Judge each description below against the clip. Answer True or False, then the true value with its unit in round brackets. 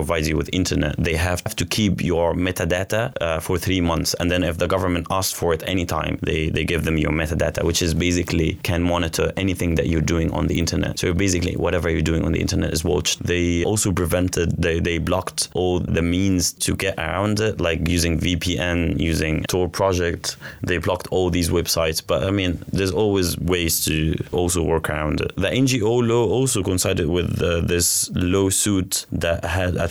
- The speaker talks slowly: False (195 wpm)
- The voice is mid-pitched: False (90 Hz)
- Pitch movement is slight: True (2.2 semitones)